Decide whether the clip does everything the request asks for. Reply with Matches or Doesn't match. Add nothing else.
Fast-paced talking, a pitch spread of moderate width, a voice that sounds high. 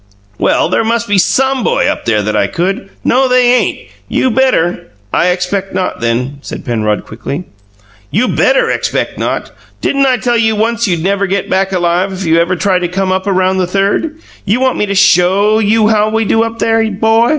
Matches